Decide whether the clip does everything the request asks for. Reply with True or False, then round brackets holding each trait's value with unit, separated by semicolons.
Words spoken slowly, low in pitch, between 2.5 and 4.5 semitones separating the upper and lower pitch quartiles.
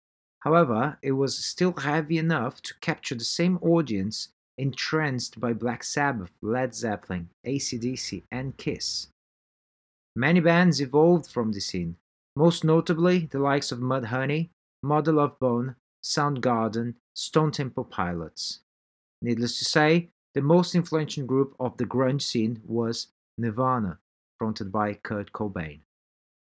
False (125 wpm; 130 Hz; 5.3 semitones)